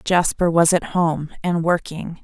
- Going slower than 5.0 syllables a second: Yes, 3.9 syllables/s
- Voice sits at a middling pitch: Yes, medium, 170 Hz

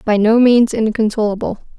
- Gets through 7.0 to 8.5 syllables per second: No, 5.0 syllables/s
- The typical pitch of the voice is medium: No, high, 220 Hz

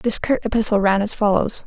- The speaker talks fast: Yes, fast, 215 wpm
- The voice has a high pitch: Yes, high, 210 Hz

